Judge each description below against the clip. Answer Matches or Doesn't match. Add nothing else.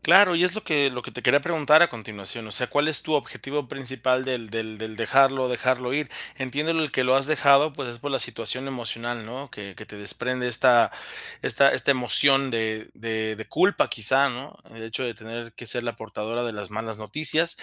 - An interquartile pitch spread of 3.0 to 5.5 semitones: Matches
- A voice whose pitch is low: Matches